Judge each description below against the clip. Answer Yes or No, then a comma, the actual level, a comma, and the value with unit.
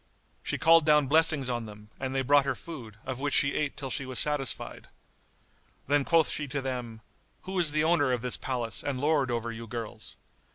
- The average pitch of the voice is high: No, low, 135 Hz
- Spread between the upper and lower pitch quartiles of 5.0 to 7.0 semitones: No, average, 3.5 semitones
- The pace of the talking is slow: No, fast, 205 wpm